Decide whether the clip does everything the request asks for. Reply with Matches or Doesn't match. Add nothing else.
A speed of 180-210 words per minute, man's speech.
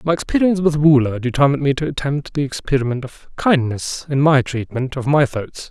Matches